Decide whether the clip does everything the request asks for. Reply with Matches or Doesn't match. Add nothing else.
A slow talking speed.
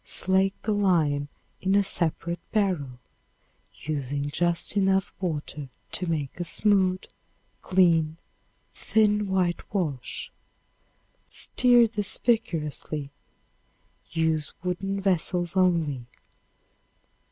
Matches